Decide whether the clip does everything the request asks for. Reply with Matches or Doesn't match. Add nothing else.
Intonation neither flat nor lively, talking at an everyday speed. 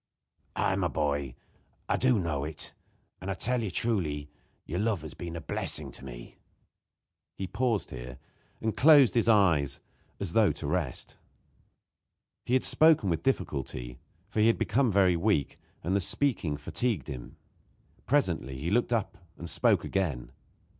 Doesn't match